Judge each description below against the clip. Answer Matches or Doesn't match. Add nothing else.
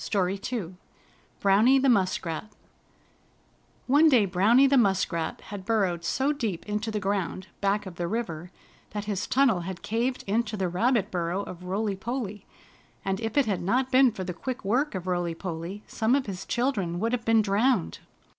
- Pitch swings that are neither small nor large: Matches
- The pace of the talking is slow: Doesn't match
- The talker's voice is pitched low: Doesn't match